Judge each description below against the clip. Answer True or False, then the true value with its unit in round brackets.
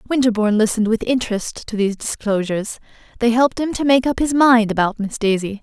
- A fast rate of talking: False (190 wpm)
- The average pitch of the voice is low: False (230 Hz)